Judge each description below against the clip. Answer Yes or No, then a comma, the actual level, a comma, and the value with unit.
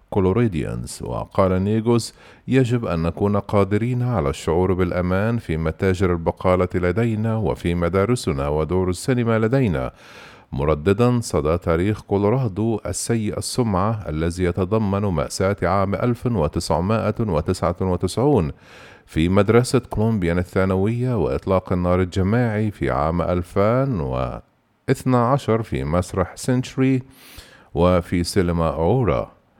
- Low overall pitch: Yes, very low, 95 Hz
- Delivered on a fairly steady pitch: No, average, 4.4 semitones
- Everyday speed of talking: Yes, average, 90 wpm